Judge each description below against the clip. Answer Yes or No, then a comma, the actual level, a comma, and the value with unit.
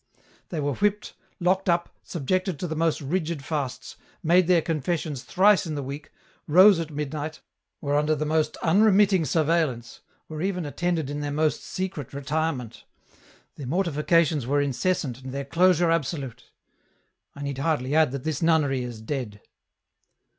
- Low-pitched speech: No, medium, 155 Hz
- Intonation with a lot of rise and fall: No, average, 3.4 semitones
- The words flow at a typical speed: Yes, average, 155 wpm